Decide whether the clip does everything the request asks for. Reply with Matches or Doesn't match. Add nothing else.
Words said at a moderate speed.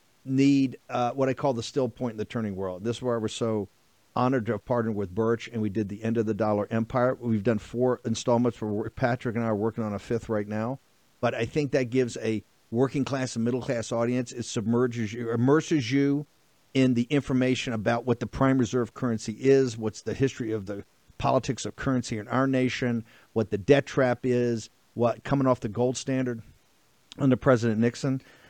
Doesn't match